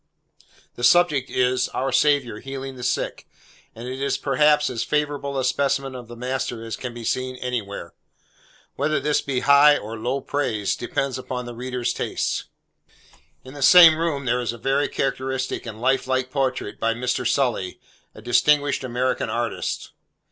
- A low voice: Yes, low, 130 Hz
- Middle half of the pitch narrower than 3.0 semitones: Yes, narrow, 2.4 semitones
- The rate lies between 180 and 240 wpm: No, average, 165 wpm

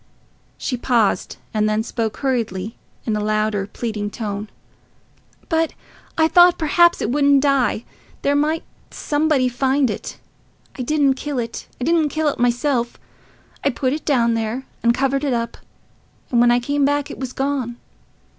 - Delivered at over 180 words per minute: No, average, 155 wpm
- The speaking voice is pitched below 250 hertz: No, very high, 255 Hz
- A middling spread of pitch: Yes, average, 3.9 semitones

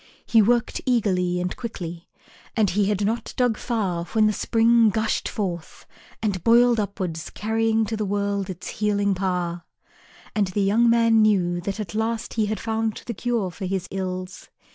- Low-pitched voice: No, high, 210 Hz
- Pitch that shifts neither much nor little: Yes, average, 3.3 semitones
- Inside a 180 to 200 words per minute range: No, average, 170 wpm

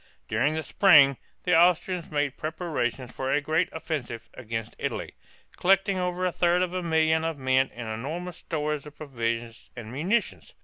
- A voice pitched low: No, medium, 155 Hz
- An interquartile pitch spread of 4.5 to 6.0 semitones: Yes, average, 5.2 semitones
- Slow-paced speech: No, average, 165 wpm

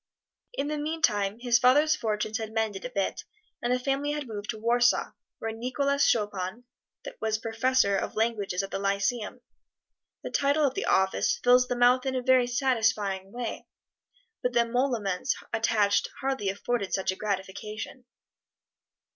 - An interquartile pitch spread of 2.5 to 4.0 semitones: Yes, average, 3.7 semitones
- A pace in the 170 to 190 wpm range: No, average, 155 wpm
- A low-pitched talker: No, high, 230 Hz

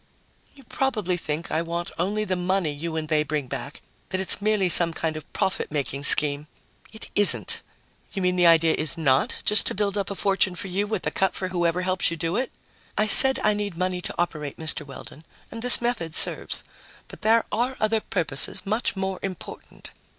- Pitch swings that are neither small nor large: Yes, average, 4.3 semitones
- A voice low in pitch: No, medium, 180 Hz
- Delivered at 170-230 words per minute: Yes, average, 200 wpm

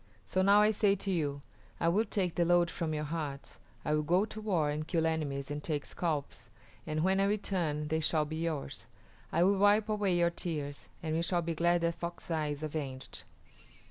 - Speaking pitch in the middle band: Yes, medium, 165 Hz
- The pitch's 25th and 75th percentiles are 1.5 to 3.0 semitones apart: No, average, 3.7 semitones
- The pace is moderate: No, fast, 210 wpm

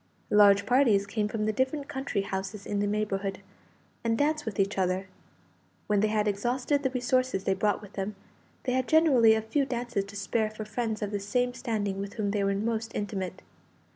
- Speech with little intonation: No, average, 3.5 semitones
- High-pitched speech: Yes, high, 215 Hz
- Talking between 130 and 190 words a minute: No, average, 200 wpm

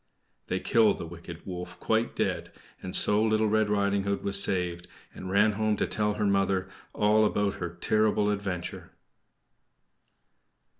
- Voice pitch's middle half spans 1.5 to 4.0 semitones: Yes, narrow, 2.6 semitones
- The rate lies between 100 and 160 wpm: Yes, average, 150 wpm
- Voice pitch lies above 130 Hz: No, low, 100 Hz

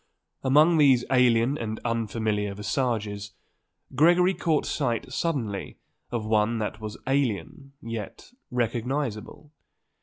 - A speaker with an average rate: No, slow, 100 wpm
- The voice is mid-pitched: No, low, 120 Hz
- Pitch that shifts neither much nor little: Yes, average, 4.3 semitones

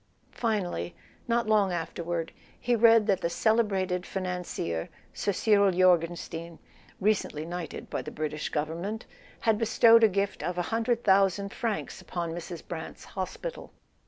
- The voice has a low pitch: No, medium, 185 Hz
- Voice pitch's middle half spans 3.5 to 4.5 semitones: Yes, average, 4.2 semitones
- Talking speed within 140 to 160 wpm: Yes, average, 145 wpm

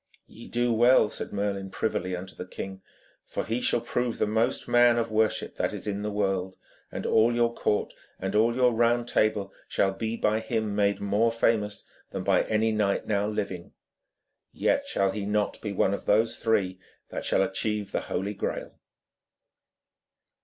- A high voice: No, low, 105 Hz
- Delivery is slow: No, average, 175 wpm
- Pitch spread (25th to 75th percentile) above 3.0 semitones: No, narrow, 2.6 semitones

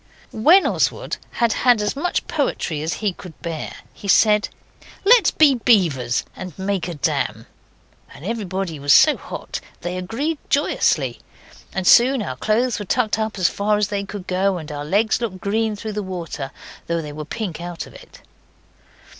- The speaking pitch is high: Yes, high, 200 Hz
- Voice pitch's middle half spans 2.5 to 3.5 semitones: No, average, 4.5 semitones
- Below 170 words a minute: No, average, 175 wpm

